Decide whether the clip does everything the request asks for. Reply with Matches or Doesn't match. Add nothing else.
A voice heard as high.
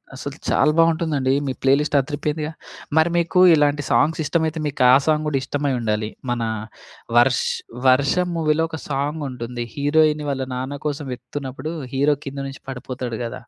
Doesn't match